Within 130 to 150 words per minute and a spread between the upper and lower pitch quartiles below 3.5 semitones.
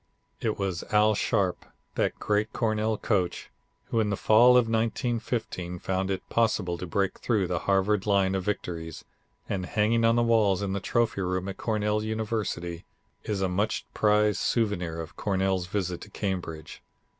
No: average, 165 wpm; average, 2.9 semitones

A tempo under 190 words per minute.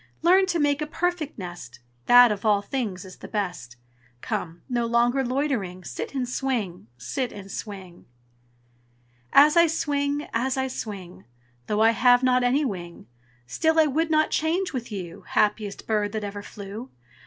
Yes: average, 165 wpm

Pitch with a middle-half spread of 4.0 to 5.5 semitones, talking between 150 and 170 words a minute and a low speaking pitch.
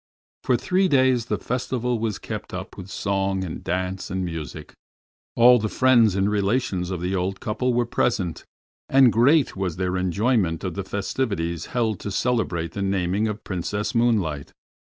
Yes: average, 4.7 semitones; average, 165 wpm; low, 100 Hz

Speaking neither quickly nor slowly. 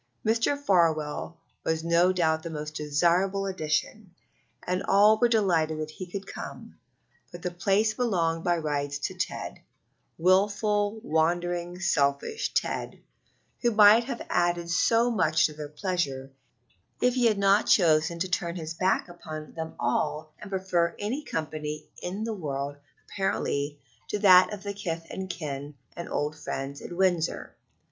Yes: average, 150 wpm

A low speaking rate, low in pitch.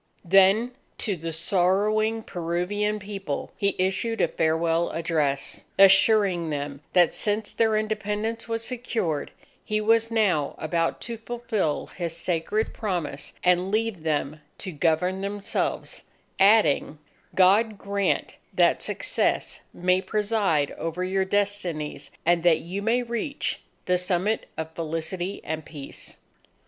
No: slow, 125 wpm; high, 190 Hz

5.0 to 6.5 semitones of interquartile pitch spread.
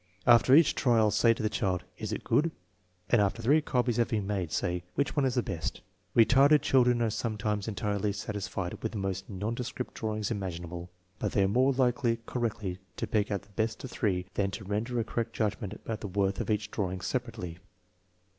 No: average, 3.6 semitones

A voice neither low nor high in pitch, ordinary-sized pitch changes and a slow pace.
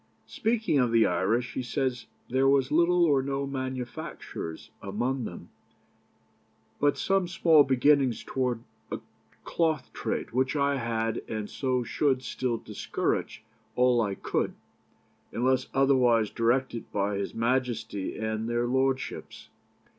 No: low, 130 Hz; average, 3.0 semitones; slow, 125 wpm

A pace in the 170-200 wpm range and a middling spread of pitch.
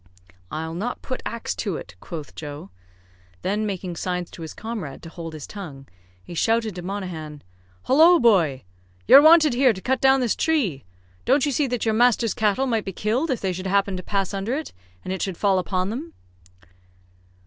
No: average, 190 wpm; wide, 5.7 semitones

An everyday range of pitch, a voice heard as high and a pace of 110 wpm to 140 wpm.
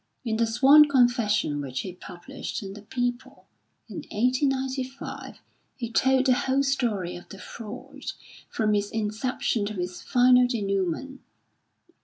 Yes: average, 4.4 semitones; high, 235 Hz; slow, 135 wpm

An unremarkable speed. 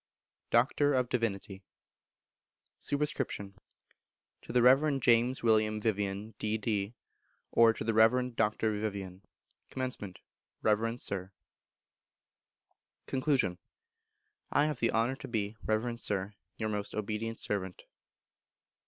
No: slow, 105 wpm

